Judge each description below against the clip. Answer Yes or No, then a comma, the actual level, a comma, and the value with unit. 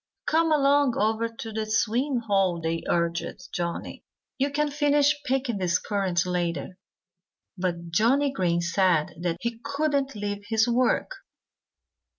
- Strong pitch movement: Yes, wide, 7.5 semitones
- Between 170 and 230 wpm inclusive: No, slow, 135 wpm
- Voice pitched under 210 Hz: No, high, 220 Hz